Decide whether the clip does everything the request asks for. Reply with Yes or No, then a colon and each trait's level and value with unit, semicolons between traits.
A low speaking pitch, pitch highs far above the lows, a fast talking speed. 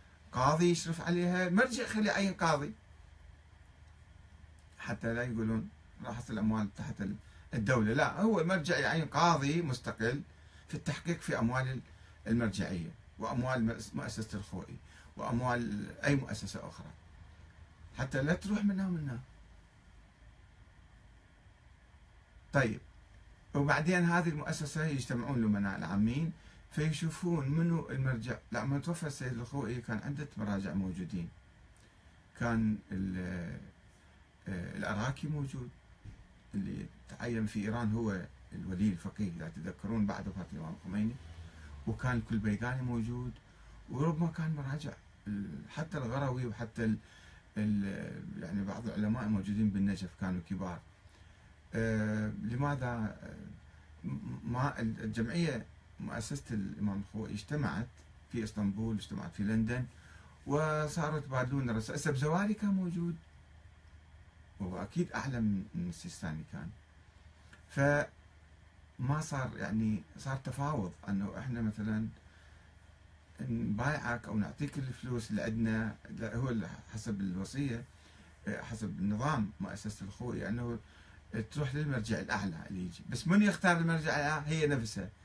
No: low, 110 Hz; wide, 6.9 semitones; average, 105 wpm